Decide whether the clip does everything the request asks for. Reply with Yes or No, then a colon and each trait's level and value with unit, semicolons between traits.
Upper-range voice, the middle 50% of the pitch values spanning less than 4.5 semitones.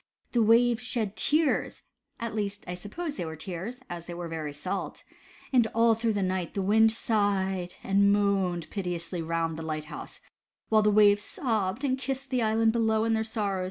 Yes: high, 205 Hz; average, 4.1 semitones